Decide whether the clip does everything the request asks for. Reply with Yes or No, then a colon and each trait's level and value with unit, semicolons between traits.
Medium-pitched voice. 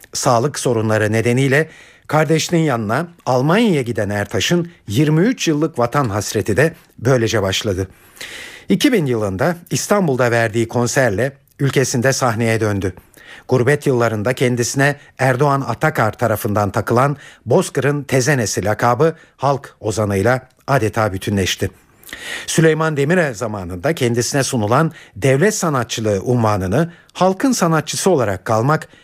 No: low, 130 Hz